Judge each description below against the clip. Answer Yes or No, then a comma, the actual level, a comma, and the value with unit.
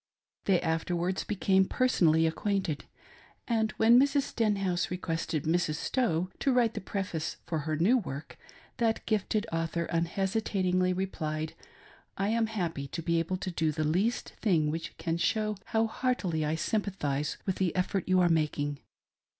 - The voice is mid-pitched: Yes, medium, 180 Hz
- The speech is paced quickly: No, average, 155 wpm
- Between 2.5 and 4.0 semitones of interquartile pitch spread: No, average, 4.5 semitones